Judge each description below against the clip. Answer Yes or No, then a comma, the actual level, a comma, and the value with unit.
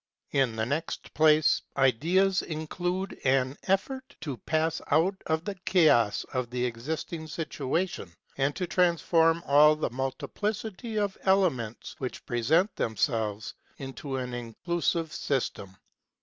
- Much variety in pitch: Yes, wide, 5.7 semitones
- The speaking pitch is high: No, medium, 155 Hz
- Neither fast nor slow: No, slow, 120 wpm